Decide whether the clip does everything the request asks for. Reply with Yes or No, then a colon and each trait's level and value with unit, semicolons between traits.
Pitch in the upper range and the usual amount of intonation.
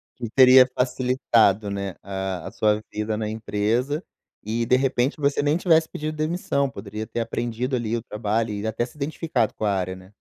No: low, 115 Hz; average, 4.0 semitones